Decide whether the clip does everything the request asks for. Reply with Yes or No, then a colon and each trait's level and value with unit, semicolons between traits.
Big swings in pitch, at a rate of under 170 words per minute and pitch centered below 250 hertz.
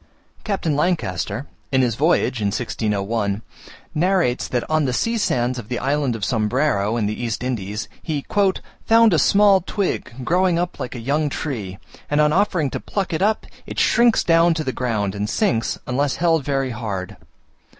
No: wide, 6.8 semitones; average, 175 wpm; low, 135 Hz